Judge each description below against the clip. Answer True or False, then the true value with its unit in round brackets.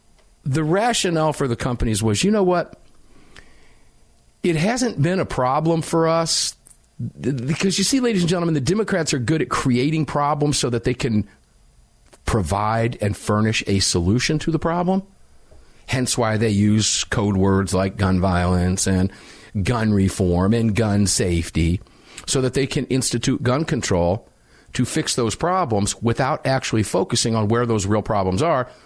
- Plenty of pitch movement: True (7.4 semitones)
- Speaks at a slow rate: False (160 wpm)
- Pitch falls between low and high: False (120 Hz)